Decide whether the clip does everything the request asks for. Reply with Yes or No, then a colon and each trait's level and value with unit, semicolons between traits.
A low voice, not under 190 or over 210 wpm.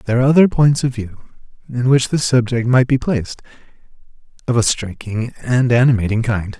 No: low, 120 Hz; average, 175 wpm